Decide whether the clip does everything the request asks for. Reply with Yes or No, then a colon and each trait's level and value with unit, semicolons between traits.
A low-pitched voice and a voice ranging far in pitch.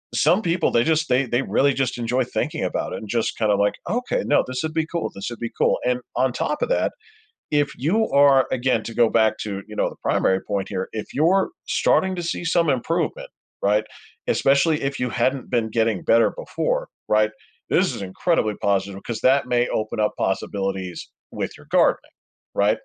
Yes: low, 125 Hz; wide, 6.4 semitones